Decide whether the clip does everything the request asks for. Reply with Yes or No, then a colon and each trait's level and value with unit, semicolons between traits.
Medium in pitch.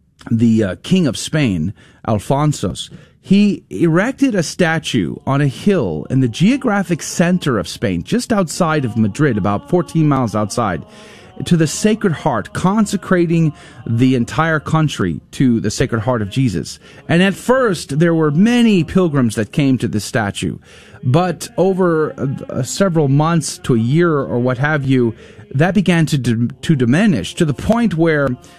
Yes: medium, 150 Hz